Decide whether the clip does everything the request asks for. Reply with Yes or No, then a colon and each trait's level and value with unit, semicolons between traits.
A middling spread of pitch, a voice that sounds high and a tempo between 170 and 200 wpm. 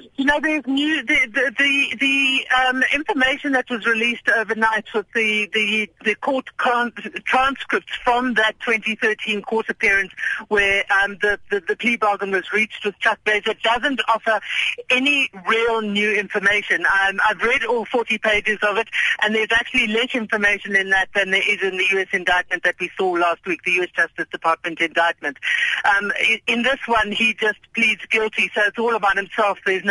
Yes: average, 3.3 semitones; high, 220 Hz; average, 180 wpm